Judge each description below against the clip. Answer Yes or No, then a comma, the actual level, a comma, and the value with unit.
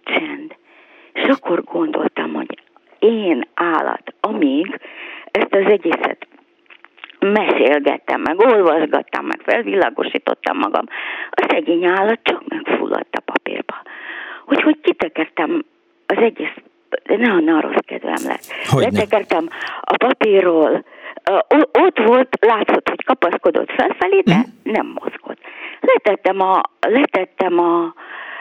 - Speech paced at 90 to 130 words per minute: Yes, slow, 105 wpm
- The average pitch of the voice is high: Yes, very high, 310 Hz